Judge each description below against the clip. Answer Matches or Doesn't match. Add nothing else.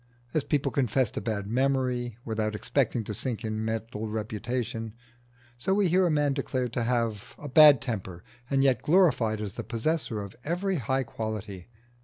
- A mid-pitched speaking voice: Doesn't match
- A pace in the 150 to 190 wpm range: Matches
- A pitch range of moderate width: Matches